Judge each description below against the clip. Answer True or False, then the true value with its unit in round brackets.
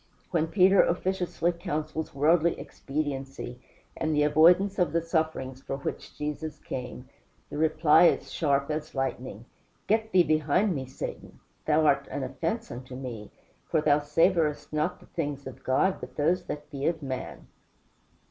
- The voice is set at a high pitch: False (155 Hz)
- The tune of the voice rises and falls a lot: False (3.5 semitones)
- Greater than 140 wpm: True (155 wpm)